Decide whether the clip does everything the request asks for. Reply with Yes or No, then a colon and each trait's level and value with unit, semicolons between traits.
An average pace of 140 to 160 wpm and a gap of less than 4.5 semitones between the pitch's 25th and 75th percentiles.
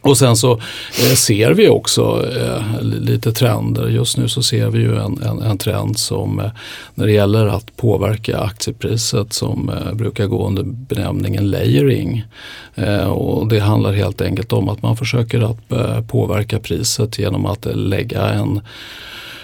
Yes: average, 145 wpm; average, 2.8 semitones